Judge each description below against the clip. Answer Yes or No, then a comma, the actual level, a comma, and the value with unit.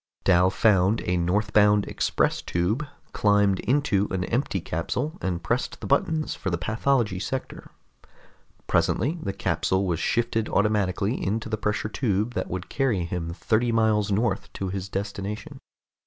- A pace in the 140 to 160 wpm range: Yes, average, 145 wpm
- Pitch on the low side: Yes, low, 105 Hz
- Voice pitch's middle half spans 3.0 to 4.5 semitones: Yes, average, 3.4 semitones